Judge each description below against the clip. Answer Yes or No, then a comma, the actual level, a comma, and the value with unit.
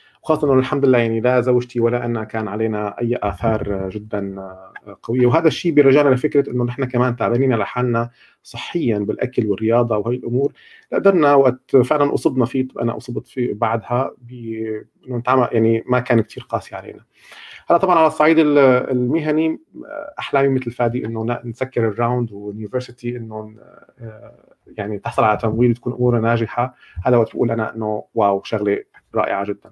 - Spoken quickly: Yes, fast, 150 wpm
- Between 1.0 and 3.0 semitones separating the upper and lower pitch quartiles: Yes, narrow, 2.6 semitones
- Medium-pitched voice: No, low, 120 Hz